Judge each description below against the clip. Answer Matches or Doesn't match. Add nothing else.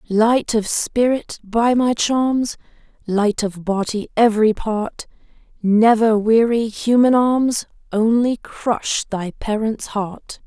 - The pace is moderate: Doesn't match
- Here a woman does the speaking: Matches